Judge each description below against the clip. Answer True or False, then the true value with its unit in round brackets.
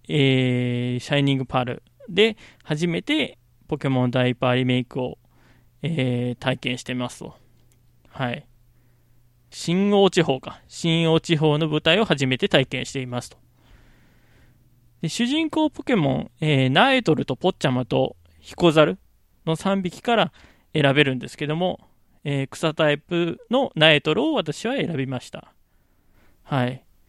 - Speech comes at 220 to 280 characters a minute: True (270 characters per minute)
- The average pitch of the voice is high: False (135 Hz)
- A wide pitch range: False (5.0 semitones)